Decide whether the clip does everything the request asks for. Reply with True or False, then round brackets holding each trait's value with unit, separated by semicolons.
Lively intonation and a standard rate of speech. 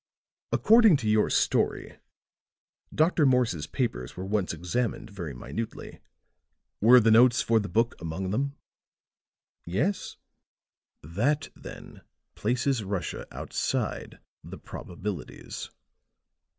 False (5.8 semitones; 100 wpm)